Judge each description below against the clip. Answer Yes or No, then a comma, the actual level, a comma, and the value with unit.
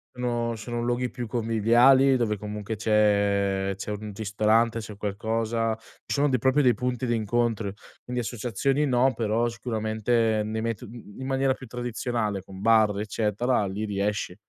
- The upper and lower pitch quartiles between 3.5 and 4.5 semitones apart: No, narrow, 2.6 semitones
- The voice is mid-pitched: No, low, 115 Hz